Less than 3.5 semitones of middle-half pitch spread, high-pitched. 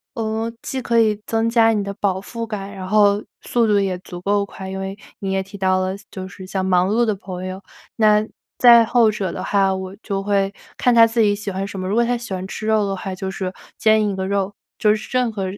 Yes: narrow, 2.4 semitones; high, 200 Hz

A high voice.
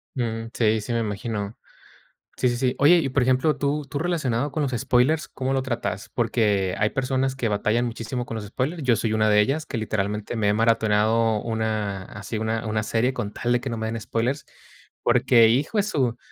No: low, 115 Hz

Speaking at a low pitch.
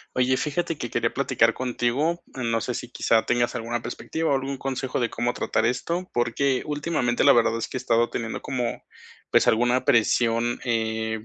Yes: low, 120 Hz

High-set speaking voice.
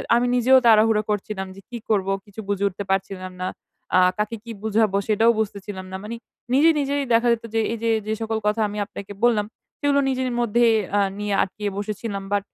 Yes: high, 215 Hz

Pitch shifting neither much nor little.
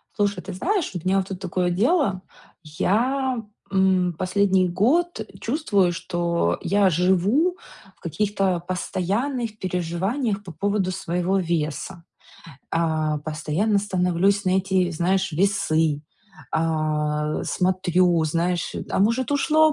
Yes: average, 3.1 semitones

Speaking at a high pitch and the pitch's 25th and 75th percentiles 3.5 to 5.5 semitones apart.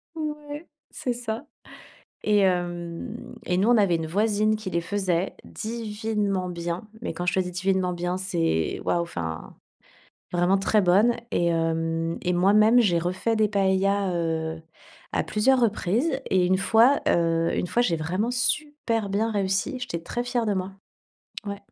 Yes: high, 195 Hz; average, 4.3 semitones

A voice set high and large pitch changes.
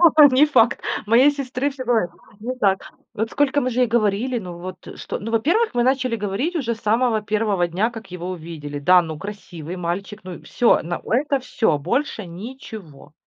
Yes: high, 220 Hz; wide, 5.8 semitones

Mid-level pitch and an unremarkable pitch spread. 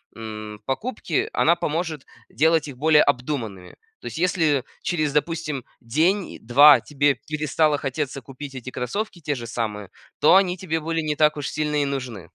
Yes: medium, 150 Hz; average, 4.0 semitones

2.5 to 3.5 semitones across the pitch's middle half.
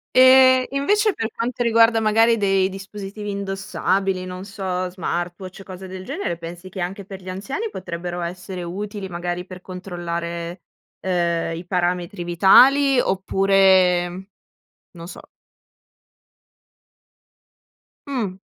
Yes: average, 2.8 semitones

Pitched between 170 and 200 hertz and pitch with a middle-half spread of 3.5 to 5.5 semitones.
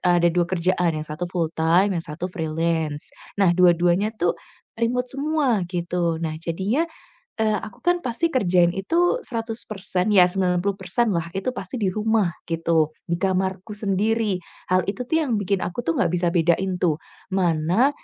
Yes: medium, 185 Hz; average, 3.9 semitones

